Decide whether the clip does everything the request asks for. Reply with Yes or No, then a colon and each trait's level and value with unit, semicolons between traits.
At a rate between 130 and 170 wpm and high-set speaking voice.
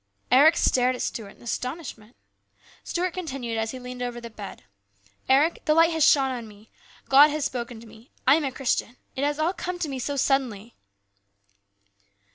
No: average, 185 wpm; very high, 260 Hz